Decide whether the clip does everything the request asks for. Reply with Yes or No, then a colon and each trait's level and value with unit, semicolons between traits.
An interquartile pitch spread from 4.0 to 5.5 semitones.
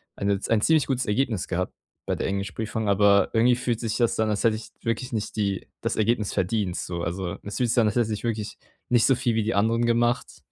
No: average, 2.8 semitones